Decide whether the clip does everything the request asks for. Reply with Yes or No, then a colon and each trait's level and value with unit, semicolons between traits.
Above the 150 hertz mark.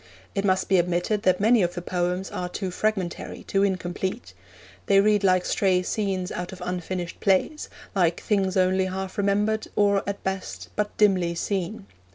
Yes: high, 190 Hz